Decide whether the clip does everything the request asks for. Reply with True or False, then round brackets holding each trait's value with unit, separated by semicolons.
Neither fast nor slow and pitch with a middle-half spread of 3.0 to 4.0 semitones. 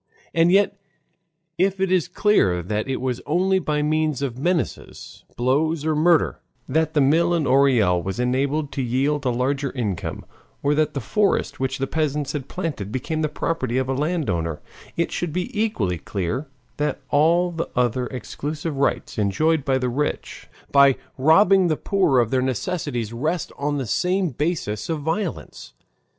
False (165 wpm; 4.5 semitones)